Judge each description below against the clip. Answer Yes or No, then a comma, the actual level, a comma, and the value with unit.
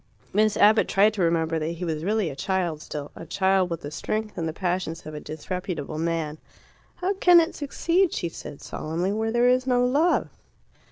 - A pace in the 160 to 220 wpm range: Yes, average, 200 wpm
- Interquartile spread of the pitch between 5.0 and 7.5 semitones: Yes, wide, 5.5 semitones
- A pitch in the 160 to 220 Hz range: Yes, medium, 185 Hz